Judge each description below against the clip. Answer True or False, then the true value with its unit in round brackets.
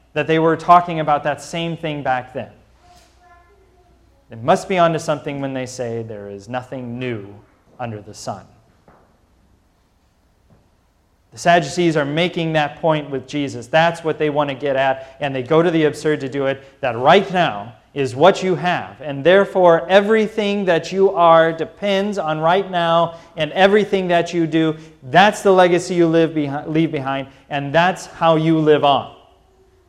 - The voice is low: False (155 Hz)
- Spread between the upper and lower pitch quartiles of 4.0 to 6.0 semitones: True (4.4 semitones)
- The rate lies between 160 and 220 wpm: True (175 wpm)